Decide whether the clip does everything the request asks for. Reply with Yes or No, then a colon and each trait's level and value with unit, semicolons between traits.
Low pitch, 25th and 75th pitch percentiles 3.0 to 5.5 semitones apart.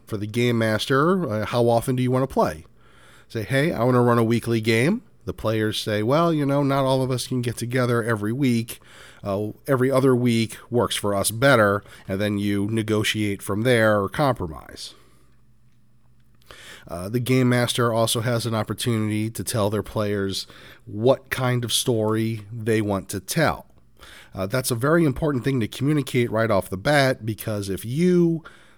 Yes: low, 115 Hz; average, 3.3 semitones